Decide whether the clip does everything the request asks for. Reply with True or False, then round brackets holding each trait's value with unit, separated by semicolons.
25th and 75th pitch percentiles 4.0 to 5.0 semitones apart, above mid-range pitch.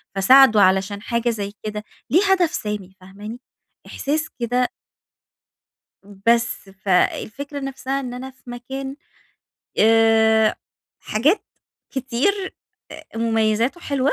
True (4.3 semitones; 235 Hz)